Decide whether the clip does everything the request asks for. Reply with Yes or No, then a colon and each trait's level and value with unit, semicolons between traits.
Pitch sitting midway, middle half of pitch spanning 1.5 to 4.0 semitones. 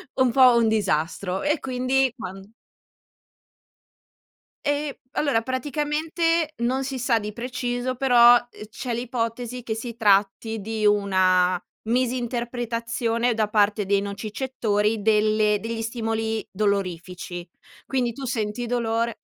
No: high, 230 Hz; average, 3.1 semitones